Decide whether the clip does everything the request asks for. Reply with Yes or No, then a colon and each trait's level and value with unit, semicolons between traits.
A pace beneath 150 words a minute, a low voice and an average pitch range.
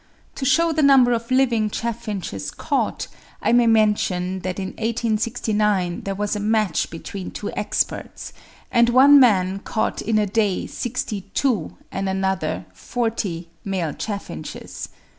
No: slow, 135 wpm; high, 210 Hz; average, 3.7 semitones